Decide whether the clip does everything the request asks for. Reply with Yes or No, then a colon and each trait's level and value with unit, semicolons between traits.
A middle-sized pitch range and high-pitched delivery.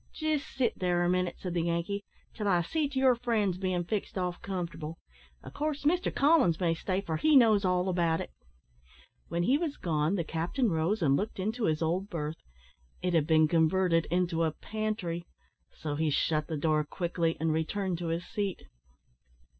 No: average, 4.3 semitones; medium, 180 Hz